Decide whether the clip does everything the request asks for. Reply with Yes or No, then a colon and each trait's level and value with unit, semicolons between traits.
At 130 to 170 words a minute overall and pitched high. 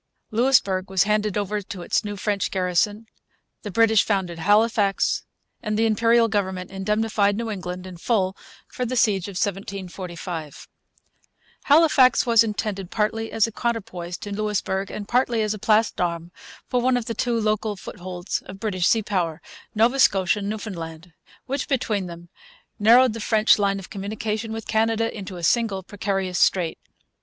Yes: average, 160 wpm; high, 205 Hz